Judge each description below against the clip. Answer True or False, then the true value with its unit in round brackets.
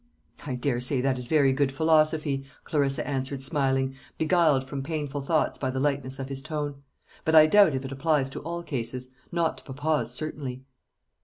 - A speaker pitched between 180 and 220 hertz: False (140 Hz)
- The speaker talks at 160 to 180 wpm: True (175 wpm)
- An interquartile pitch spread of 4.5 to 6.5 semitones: False (2.6 semitones)